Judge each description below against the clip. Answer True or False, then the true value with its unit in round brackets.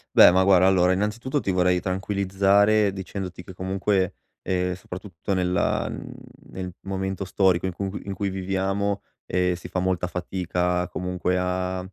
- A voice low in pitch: True (95 Hz)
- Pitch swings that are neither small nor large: False (1.2 semitones)